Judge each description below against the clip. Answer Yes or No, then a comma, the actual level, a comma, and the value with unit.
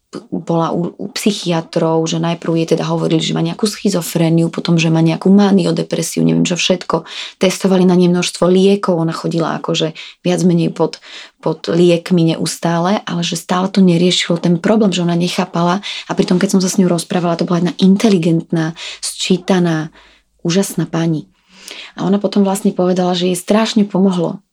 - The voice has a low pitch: No, medium, 175 Hz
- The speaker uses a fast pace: Yes, fast, 170 wpm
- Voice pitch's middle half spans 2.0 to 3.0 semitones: Yes, narrow, 2.4 semitones